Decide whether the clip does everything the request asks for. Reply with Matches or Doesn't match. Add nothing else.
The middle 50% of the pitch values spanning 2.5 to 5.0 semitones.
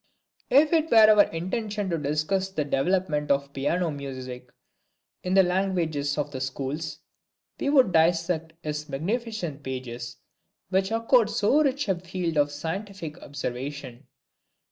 Doesn't match